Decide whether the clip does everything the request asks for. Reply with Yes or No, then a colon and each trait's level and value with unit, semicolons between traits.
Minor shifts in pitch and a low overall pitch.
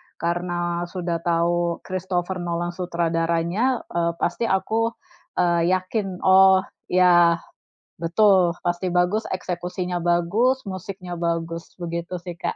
No: narrow, 1.6 semitones; medium, 175 Hz